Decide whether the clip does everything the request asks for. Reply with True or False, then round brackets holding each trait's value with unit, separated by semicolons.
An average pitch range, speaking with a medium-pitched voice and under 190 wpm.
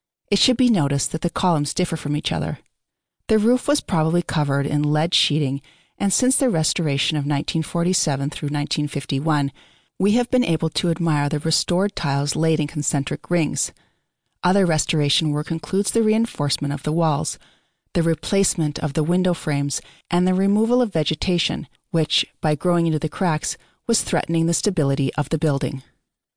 True (3.5 semitones; 160 Hz; 165 wpm)